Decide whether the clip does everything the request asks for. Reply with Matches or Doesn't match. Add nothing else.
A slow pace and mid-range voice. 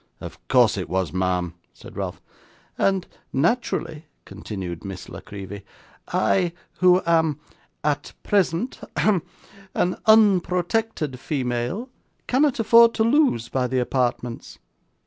Matches